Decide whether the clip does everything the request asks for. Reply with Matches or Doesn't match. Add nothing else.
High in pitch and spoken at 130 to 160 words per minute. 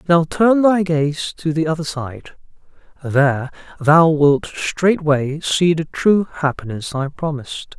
Doesn't match